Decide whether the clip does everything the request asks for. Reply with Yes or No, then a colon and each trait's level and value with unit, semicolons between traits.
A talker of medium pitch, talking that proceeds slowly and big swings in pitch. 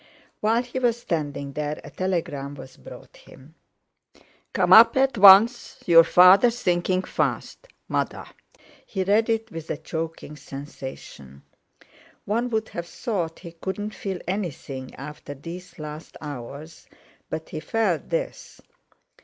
Yes: medium, 175 Hz; slow, 130 wpm; wide, 6.1 semitones